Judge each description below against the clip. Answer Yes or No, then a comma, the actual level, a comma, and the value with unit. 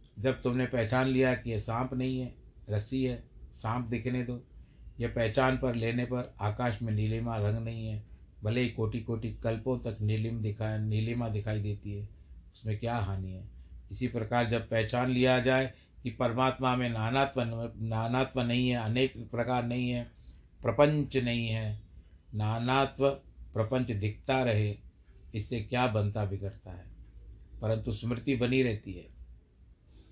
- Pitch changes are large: No, average, 2.9 semitones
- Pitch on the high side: No, low, 115 Hz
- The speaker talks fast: No, average, 150 wpm